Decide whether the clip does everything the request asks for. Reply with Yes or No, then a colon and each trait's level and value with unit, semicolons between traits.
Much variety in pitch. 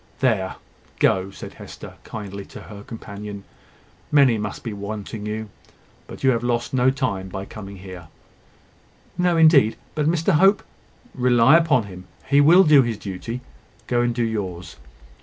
No: average, 5.0 semitones